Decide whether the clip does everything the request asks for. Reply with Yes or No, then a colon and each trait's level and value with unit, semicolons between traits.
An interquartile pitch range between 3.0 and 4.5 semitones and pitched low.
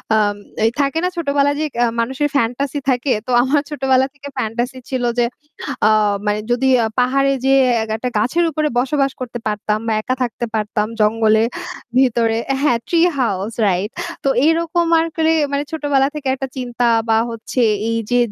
No: average, 3.8 semitones; very high, 255 Hz